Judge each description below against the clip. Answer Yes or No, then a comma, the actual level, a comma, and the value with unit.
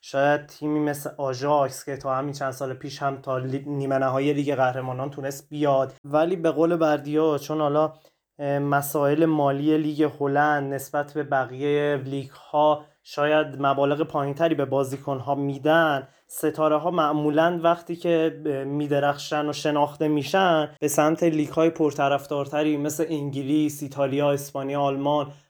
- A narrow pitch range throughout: Yes, narrow, 1.6 semitones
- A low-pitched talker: No, medium, 145 Hz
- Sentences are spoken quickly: No, average, 140 wpm